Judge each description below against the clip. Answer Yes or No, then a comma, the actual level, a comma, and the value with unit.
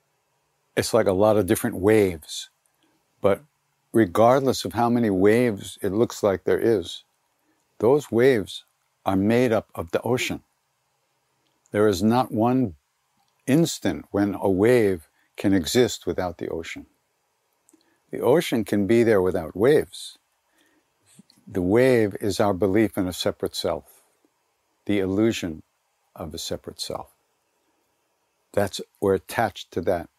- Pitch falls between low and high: No, low, 110 Hz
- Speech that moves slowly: Yes, slow, 130 wpm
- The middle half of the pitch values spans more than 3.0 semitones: Yes, average, 3.4 semitones